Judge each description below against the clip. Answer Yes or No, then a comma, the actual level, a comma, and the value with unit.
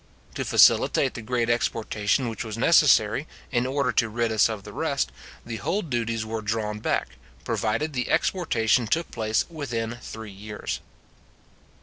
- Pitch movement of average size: No, narrow, 2.3 semitones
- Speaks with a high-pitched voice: No, low, 115 Hz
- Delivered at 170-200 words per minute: No, average, 150 wpm